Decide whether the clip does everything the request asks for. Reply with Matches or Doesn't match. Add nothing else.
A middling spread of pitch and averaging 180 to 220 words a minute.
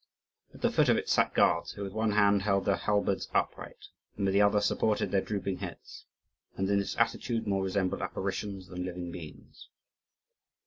Doesn't match